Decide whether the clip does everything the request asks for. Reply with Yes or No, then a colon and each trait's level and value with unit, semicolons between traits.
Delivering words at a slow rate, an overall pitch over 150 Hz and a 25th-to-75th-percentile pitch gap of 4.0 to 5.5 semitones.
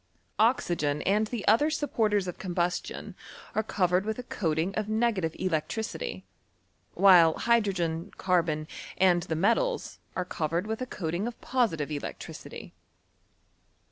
Yes: slow, 125 wpm; high, 190 Hz; average, 4.7 semitones